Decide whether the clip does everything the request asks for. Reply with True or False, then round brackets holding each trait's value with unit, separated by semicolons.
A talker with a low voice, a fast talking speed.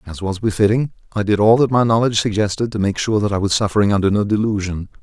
True (105 Hz; 240 wpm)